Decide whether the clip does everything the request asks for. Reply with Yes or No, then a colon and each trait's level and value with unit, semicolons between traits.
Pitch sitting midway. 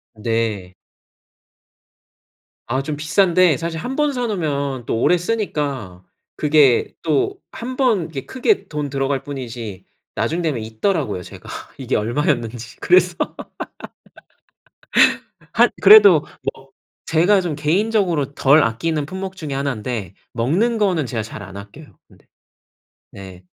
Yes: medium, 145 Hz